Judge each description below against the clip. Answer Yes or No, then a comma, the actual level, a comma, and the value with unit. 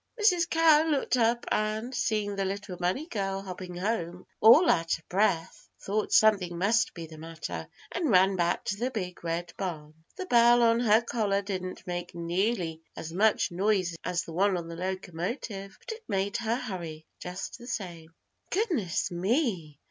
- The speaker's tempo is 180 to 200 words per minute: No, average, 170 wpm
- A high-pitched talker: Yes, high, 195 Hz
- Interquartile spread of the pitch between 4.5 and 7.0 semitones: Yes, average, 4.8 semitones